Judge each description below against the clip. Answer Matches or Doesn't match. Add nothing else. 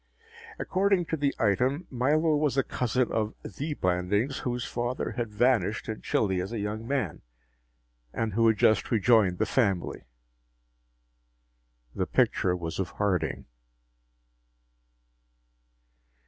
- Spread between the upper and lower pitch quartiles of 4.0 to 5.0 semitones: Matches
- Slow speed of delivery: Matches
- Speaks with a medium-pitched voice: Doesn't match